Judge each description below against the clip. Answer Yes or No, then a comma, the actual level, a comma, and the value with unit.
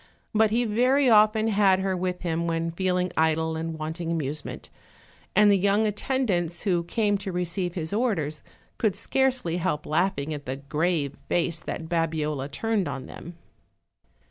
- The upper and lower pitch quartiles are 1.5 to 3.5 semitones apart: No, average, 4.5 semitones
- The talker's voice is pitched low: No, medium, 175 Hz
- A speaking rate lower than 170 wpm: Yes, average, 155 wpm